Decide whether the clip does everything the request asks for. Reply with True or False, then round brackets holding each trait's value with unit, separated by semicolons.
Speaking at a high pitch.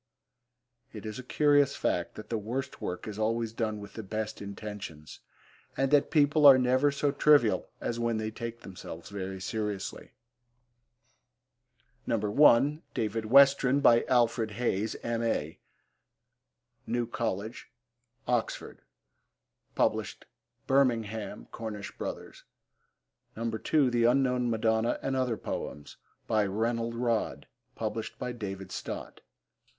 False (115 Hz)